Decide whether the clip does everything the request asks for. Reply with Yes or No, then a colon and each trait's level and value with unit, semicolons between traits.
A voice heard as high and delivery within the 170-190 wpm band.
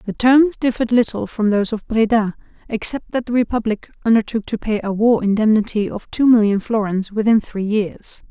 Yes: high, 220 Hz; average, 180 wpm